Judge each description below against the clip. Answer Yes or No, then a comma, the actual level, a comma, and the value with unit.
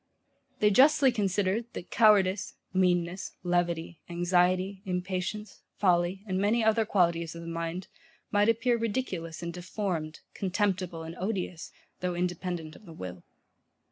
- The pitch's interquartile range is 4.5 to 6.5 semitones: No, average, 3.1 semitones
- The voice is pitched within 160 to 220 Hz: Yes, medium, 185 Hz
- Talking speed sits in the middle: No, slow, 130 wpm